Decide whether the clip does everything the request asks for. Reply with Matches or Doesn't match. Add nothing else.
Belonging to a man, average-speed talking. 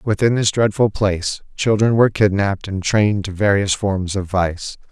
Matches